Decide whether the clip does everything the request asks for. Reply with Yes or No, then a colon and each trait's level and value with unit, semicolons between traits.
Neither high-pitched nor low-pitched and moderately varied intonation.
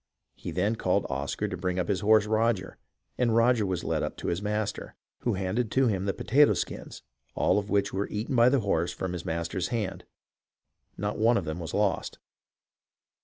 No: low, 105 Hz; average, 3.6 semitones